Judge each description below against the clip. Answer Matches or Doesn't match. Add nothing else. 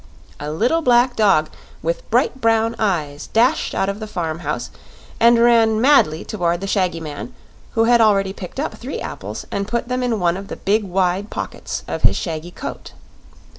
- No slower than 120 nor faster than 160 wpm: Doesn't match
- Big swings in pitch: Doesn't match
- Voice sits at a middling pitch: Doesn't match